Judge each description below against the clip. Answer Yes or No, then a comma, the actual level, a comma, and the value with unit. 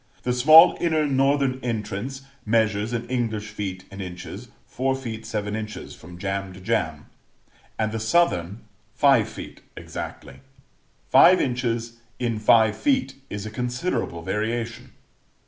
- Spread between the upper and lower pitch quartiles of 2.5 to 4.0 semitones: Yes, average, 3.7 semitones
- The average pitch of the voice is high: No, low, 115 Hz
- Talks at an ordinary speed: No, slow, 130 wpm